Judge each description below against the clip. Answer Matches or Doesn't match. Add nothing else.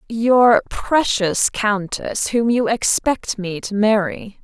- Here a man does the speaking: Doesn't match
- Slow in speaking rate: Matches